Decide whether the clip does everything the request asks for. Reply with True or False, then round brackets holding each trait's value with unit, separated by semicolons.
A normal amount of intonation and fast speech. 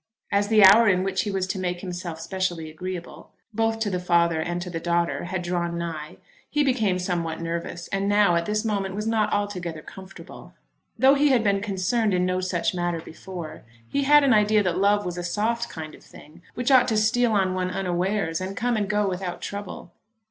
True (3.3 semitones; 210 wpm)